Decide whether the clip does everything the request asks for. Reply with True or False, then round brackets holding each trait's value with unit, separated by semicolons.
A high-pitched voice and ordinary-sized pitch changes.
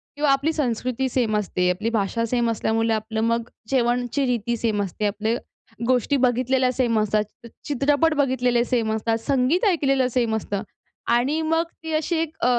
True (245 Hz; 3.4 semitones)